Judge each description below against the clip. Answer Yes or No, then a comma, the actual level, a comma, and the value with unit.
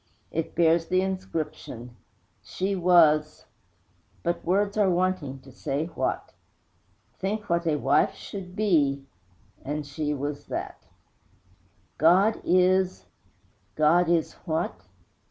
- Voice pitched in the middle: Yes, medium, 170 Hz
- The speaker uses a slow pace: Yes, slow, 110 wpm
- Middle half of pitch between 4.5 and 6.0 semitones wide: No, average, 3.8 semitones